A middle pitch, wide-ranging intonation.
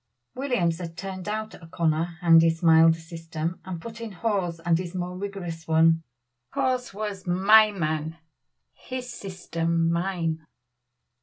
No: medium, 175 Hz; average, 3.3 semitones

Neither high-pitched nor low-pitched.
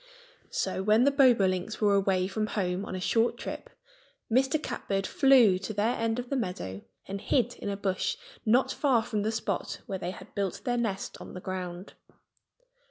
No: high, 205 Hz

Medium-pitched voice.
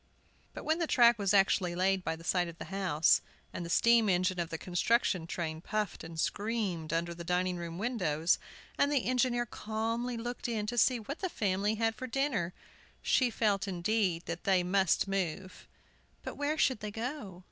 No: high, 195 Hz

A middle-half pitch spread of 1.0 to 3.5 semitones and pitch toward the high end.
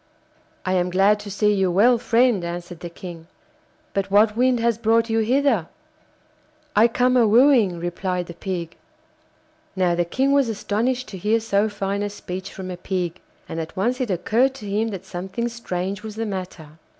No: average, 4.1 semitones; high, 205 Hz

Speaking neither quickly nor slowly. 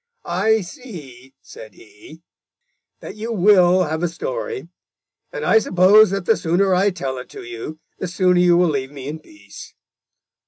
Yes: average, 165 wpm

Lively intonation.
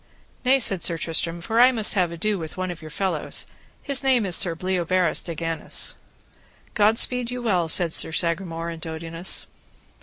No: average, 4.4 semitones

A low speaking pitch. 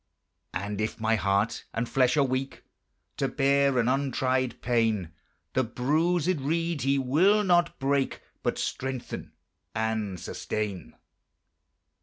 Yes: low, 130 Hz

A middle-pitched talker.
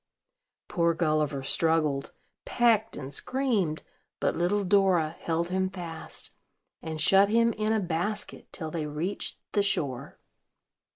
Yes: medium, 175 Hz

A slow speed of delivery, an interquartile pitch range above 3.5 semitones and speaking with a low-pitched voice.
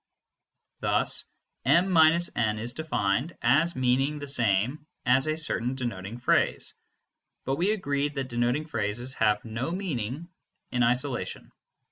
Yes: slow, 130 wpm; average, 4.5 semitones; low, 130 Hz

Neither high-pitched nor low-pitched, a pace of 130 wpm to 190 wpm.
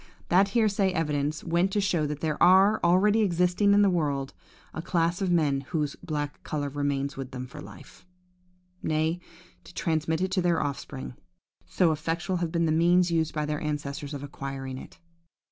Yes: medium, 165 Hz; average, 175 wpm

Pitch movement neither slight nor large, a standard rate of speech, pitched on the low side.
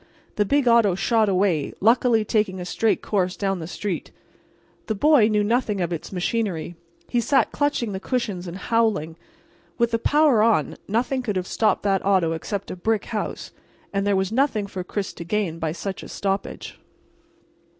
No: average, 3.6 semitones; average, 180 wpm; high, 205 Hz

